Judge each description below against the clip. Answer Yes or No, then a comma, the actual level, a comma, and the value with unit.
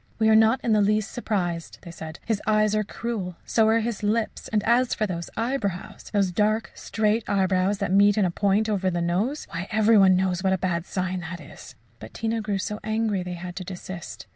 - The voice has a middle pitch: No, high, 205 Hz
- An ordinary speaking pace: No, fast, 220 wpm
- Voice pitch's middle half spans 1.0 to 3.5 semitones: Yes, average, 3.0 semitones